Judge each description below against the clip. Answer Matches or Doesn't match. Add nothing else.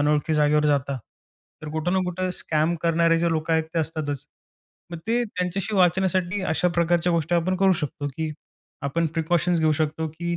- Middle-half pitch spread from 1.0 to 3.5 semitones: Matches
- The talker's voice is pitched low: Doesn't match